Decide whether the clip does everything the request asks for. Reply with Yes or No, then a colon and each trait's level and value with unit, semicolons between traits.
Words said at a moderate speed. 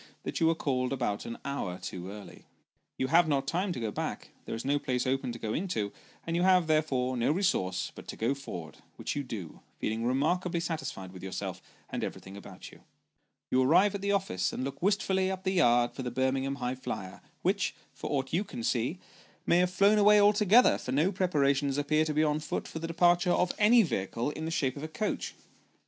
No: fast, 215 wpm